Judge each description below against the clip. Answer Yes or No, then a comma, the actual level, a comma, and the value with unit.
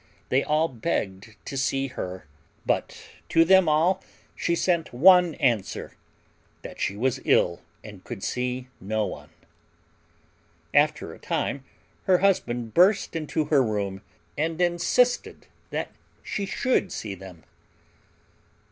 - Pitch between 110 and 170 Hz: Yes, low, 135 Hz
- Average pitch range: No, wide, 8.0 semitones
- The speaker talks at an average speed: No, slow, 125 wpm